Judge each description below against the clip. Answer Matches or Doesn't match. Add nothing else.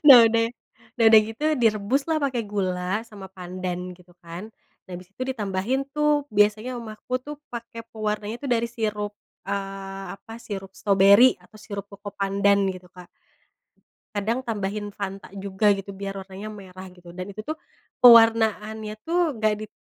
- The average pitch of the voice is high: Matches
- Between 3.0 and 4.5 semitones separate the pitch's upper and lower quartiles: Doesn't match